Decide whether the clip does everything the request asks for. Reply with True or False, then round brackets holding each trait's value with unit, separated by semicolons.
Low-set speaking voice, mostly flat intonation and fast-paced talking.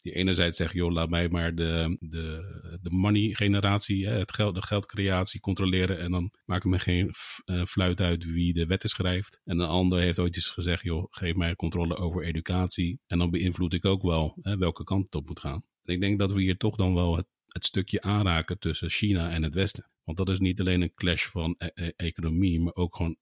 True (90 Hz; 2.1 semitones; 215 wpm)